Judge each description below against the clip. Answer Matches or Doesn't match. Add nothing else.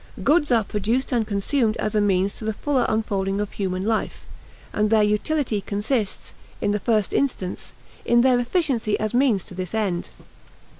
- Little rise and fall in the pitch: Doesn't match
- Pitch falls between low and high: Doesn't match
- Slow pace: Doesn't match